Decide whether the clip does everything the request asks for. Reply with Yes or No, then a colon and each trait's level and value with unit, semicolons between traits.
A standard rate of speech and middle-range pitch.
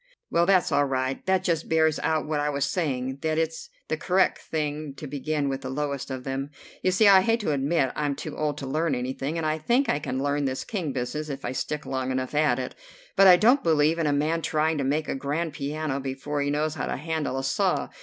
No: fast, 245 wpm; medium, 150 Hz